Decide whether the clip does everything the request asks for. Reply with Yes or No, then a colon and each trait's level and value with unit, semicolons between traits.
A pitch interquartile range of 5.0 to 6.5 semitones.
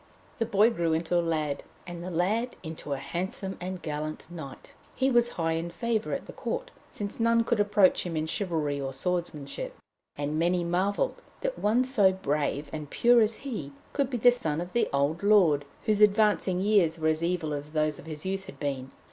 Yes: wide, 5.4 semitones